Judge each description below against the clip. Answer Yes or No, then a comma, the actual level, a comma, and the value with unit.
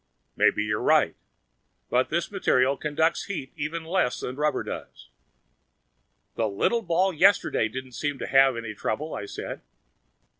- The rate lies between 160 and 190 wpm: No, average, 145 wpm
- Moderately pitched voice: Yes, medium, 145 Hz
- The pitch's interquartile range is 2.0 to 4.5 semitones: No, average, 5.0 semitones